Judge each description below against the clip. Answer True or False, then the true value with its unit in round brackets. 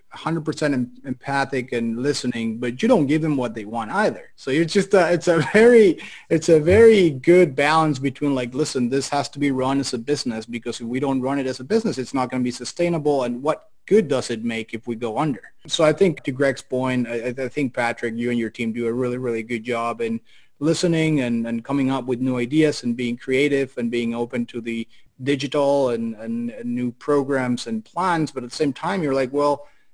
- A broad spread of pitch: False (4.0 semitones)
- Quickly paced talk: True (230 wpm)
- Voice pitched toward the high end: False (130 Hz)